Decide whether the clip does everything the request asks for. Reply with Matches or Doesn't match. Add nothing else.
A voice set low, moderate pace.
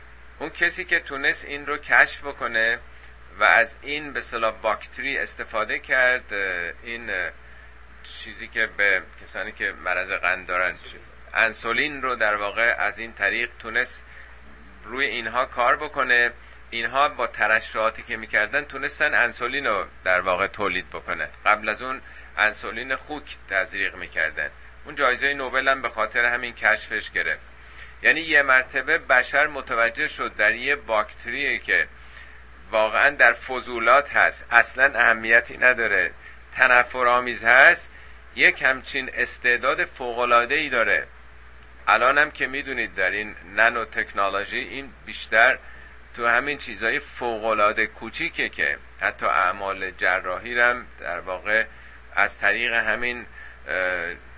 Matches